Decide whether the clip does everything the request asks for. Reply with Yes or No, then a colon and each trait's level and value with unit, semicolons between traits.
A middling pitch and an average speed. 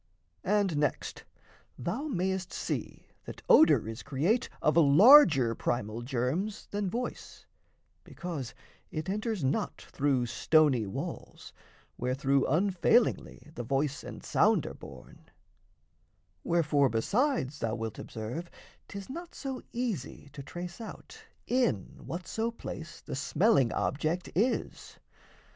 No: medium, 160 Hz; slow, 115 wpm